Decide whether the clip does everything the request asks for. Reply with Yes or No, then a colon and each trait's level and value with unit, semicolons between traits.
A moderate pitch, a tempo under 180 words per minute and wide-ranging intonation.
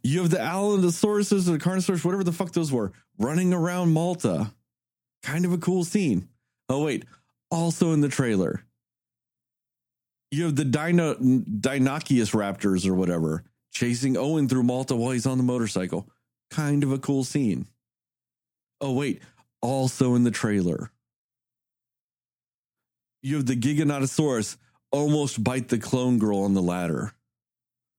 No: low, 130 Hz; average, 140 wpm; wide, 6.6 semitones